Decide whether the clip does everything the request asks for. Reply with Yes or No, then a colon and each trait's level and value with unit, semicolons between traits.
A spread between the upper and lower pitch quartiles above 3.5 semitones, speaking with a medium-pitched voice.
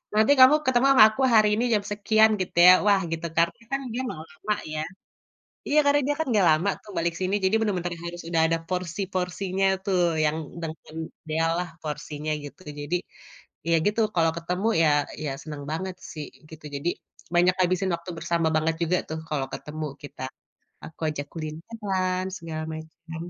Yes: average, 3.9 semitones; medium, 175 Hz